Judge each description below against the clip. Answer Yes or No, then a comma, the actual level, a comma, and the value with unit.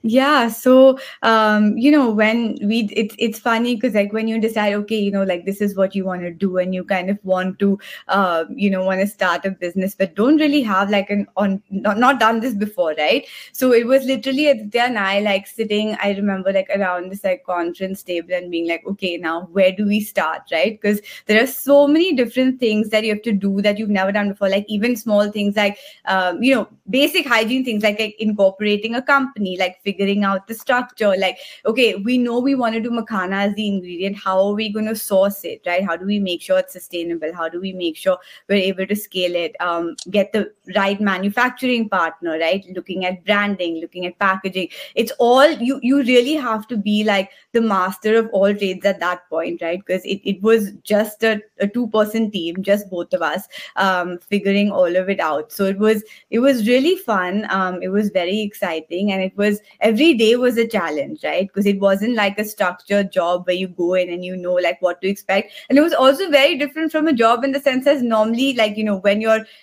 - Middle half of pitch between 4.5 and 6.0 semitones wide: No, average, 3.2 semitones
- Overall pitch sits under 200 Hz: No, high, 205 Hz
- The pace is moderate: No, fast, 230 wpm